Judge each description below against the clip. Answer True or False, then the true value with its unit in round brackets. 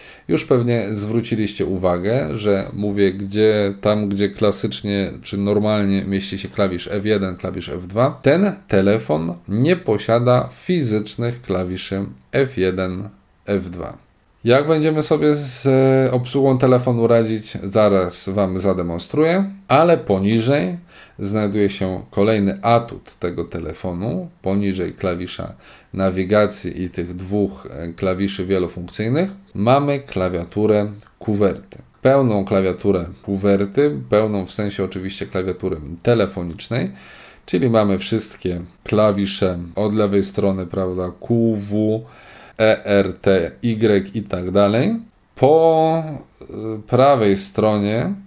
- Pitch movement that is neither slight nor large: True (3.7 semitones)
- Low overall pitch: True (105 Hz)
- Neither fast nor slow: False (105 wpm)